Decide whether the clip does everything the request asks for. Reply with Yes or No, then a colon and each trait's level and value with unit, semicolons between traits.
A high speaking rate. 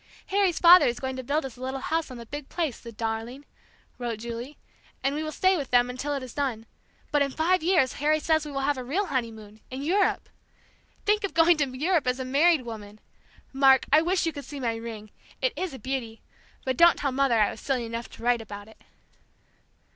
Yes: fast, 225 wpm